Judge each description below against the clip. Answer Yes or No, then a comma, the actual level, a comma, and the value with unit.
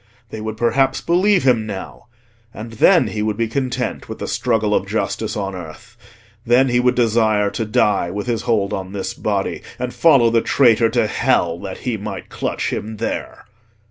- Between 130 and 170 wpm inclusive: No, average, 180 wpm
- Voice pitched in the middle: No, low, 110 Hz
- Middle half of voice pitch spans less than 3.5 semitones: Yes, average, 3.1 semitones